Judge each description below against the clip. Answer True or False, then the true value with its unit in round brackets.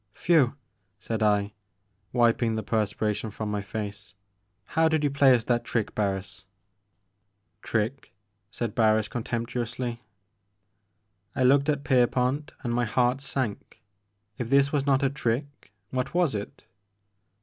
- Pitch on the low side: True (120 Hz)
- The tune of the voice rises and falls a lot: False (4.1 semitones)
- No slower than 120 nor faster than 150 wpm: True (140 wpm)